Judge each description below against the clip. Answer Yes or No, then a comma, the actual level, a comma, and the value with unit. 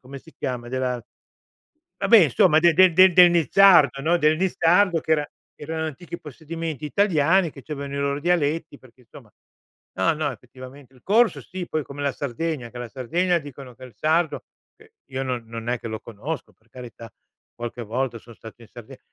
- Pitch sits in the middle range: Yes, medium, 145 Hz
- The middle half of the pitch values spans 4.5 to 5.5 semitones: Yes, average, 5.0 semitones